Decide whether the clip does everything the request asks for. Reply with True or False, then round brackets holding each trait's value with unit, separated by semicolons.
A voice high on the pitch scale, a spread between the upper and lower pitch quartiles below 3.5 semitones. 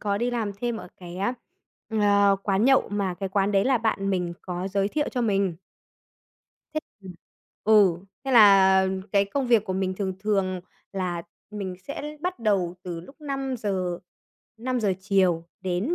True (200 Hz; 3.1 semitones)